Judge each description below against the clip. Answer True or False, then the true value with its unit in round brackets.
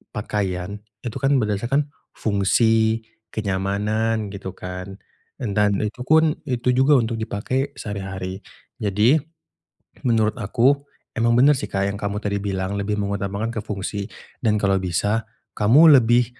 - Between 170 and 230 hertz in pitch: False (105 Hz)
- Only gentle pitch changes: False (3.0 semitones)